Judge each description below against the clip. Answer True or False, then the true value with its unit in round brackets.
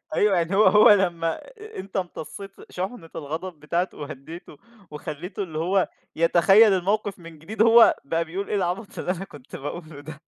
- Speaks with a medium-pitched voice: True (175 Hz)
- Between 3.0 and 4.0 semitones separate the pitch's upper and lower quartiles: True (3.5 semitones)